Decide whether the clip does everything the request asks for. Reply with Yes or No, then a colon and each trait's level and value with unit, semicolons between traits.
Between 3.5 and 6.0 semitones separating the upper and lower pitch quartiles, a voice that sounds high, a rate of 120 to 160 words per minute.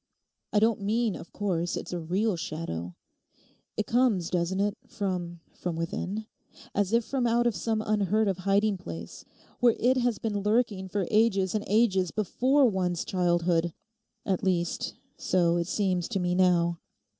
Yes: average, 3.8 semitones; high, 195 Hz; average, 155 wpm